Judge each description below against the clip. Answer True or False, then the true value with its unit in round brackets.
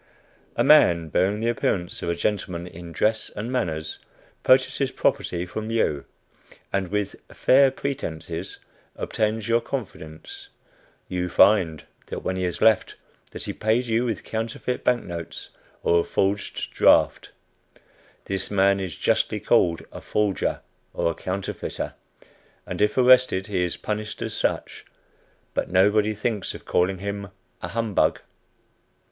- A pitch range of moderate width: True (4.1 semitones)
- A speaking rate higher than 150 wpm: False (135 wpm)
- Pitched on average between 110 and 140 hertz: False (100 Hz)